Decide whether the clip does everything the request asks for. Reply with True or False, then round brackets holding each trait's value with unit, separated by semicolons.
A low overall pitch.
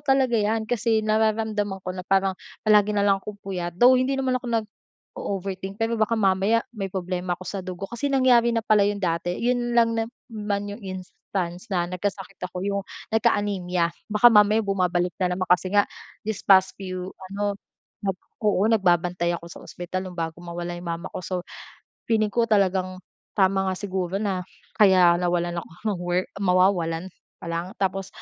False (195 Hz)